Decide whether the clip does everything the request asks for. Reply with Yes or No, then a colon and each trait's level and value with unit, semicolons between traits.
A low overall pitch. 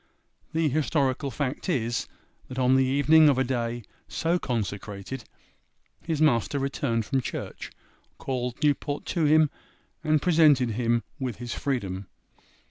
Yes: low, 130 Hz